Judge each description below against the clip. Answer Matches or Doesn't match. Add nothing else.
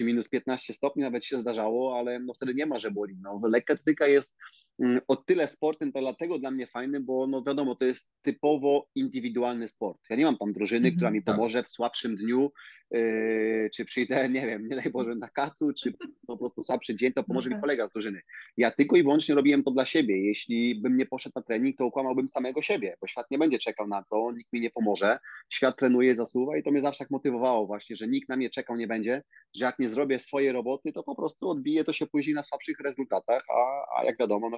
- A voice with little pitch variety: Doesn't match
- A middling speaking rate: Doesn't match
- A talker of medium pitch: Doesn't match